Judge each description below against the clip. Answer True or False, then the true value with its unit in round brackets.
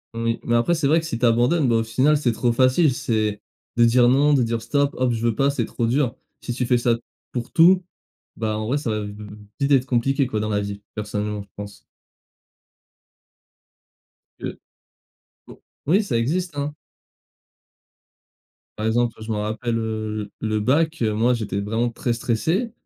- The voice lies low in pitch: True (120 Hz)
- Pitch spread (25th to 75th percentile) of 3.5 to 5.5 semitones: True (4.1 semitones)